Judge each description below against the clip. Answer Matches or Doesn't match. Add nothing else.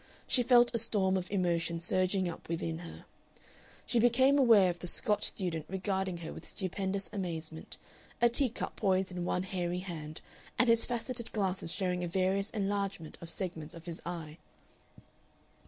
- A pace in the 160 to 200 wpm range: Matches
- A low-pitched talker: Doesn't match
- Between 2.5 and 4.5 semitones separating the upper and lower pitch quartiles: Matches